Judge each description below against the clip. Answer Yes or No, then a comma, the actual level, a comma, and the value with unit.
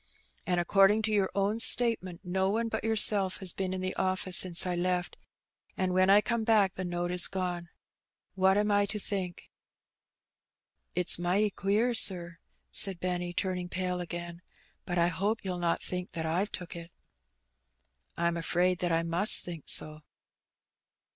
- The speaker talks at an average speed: Yes, average, 165 wpm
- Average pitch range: No, narrow, 2.2 semitones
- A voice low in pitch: No, medium, 185 Hz